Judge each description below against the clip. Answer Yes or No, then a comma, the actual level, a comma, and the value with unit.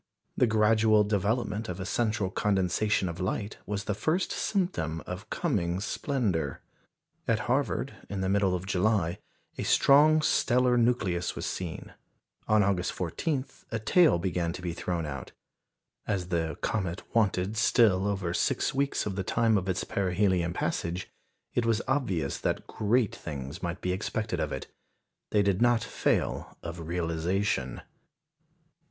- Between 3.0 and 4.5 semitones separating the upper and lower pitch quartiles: Yes, average, 3.9 semitones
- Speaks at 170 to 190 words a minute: No, average, 145 wpm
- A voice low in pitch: Yes, low, 100 Hz